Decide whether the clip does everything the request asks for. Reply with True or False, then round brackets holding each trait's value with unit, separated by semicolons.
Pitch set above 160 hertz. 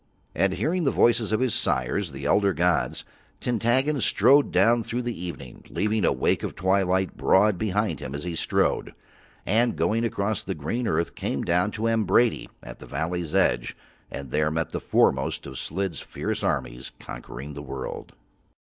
False (95 Hz)